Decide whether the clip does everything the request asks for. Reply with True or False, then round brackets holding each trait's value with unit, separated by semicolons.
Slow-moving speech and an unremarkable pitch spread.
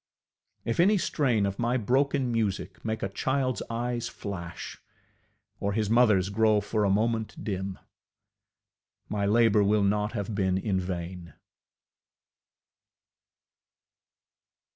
True (115 wpm; 3.0 semitones)